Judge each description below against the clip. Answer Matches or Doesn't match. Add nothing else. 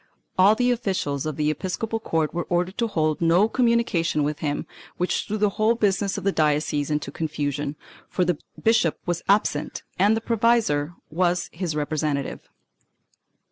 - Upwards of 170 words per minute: Doesn't match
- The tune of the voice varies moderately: Doesn't match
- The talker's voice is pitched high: Doesn't match